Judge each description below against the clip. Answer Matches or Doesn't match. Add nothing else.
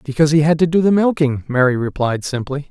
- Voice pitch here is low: Doesn't match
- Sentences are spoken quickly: Matches